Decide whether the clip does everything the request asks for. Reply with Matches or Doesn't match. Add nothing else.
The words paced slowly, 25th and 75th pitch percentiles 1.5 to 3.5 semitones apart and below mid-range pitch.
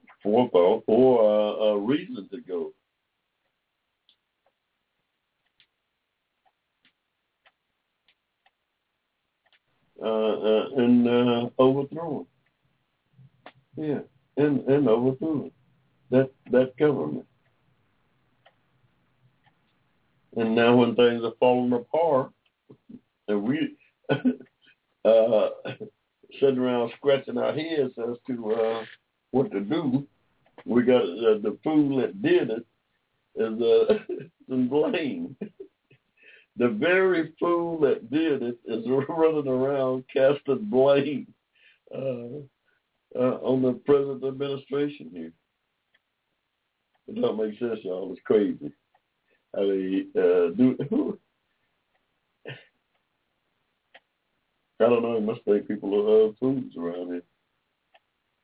Doesn't match